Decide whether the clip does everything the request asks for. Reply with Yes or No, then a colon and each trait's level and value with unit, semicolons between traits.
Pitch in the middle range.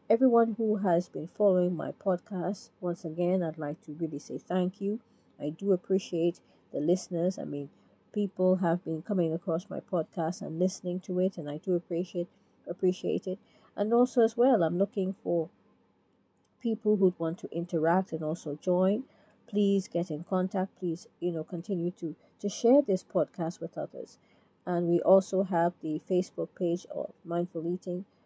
Yes: medium, 180 Hz